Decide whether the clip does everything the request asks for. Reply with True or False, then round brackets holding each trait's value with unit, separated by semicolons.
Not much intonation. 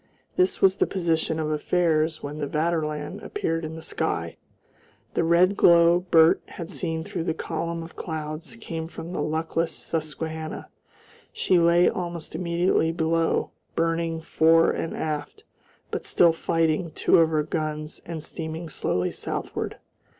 True (1.3 semitones)